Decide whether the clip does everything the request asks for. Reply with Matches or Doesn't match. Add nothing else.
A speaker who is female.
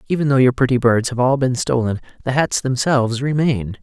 Doesn't match